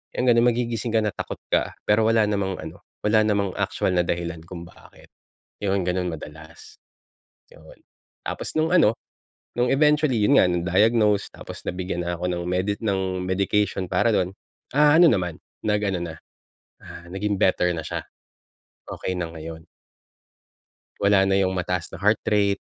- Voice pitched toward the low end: Yes, very low, 95 Hz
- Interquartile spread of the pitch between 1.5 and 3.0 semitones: No, average, 3.5 semitones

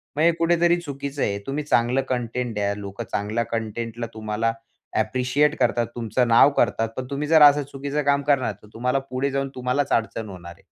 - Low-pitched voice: Yes, low, 125 Hz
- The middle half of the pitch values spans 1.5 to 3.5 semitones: No, average, 3.9 semitones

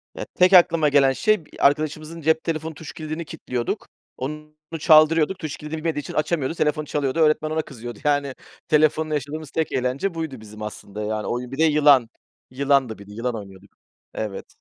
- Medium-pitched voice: Yes, medium, 150 Hz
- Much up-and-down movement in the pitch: No, average, 3.7 semitones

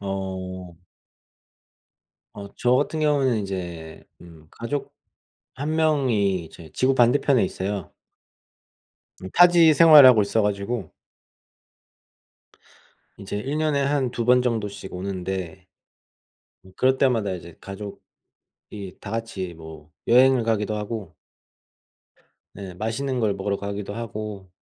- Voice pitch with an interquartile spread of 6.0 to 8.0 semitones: No, average, 5.2 semitones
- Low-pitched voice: Yes, low, 105 Hz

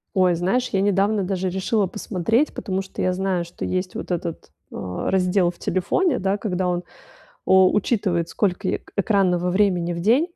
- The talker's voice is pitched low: No, high, 190 Hz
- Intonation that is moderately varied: No, narrow, 2.2 semitones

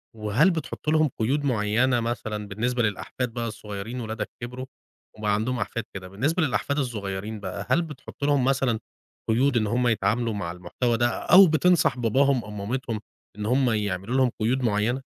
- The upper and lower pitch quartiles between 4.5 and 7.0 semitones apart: No, average, 3.8 semitones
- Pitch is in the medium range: No, low, 120 Hz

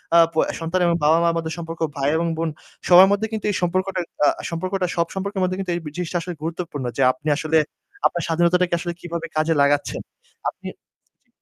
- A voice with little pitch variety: Yes, narrow, 2.0 semitones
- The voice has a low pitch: No, medium, 170 Hz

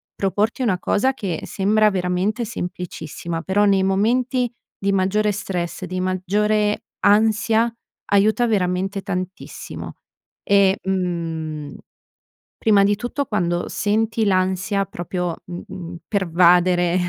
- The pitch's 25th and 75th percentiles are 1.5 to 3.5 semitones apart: Yes, average, 2.8 semitones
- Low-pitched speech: No, high, 195 Hz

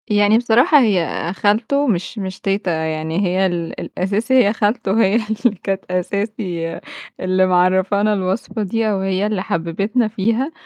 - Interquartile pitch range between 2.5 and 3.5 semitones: Yes, average, 3.0 semitones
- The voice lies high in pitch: Yes, high, 200 Hz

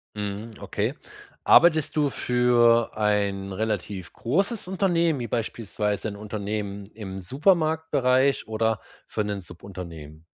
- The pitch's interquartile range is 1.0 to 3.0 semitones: No, average, 5.1 semitones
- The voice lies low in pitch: Yes, low, 110 Hz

